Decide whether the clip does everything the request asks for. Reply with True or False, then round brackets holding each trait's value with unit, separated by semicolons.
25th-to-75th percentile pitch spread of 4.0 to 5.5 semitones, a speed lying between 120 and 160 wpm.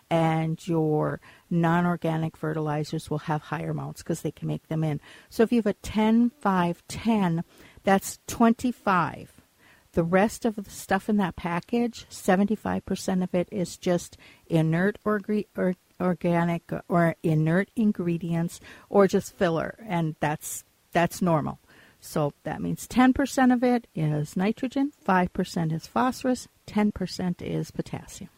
True (4.6 semitones; 135 wpm)